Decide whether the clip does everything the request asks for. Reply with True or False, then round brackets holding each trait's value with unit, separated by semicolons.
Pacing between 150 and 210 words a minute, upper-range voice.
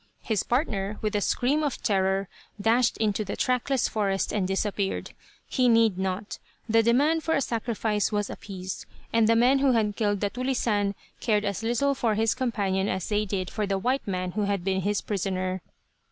True (185 wpm; 210 Hz)